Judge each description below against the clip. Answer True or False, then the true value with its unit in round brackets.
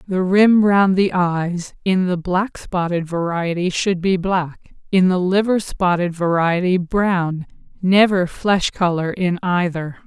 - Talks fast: False (135 wpm)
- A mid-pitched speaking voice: True (180 Hz)